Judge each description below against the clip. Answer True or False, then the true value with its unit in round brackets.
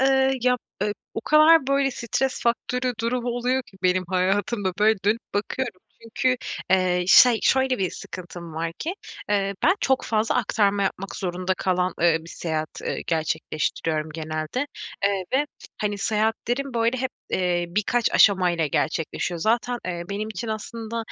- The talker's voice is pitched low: False (210 Hz)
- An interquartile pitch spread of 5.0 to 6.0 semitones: True (5.3 semitones)